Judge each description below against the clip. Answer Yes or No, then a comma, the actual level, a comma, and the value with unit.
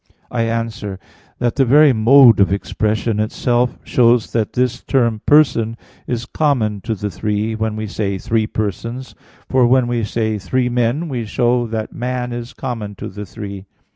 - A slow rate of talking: No, average, 170 wpm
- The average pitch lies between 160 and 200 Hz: No, low, 115 Hz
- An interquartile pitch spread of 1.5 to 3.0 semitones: Yes, narrow, 2.4 semitones